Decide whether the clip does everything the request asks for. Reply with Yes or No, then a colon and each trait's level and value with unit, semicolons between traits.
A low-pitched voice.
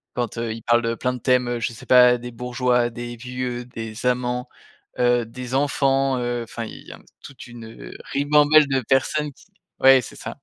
Yes: low, 125 Hz